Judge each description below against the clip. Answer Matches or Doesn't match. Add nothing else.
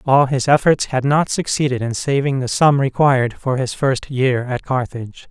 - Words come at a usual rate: Matches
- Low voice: Matches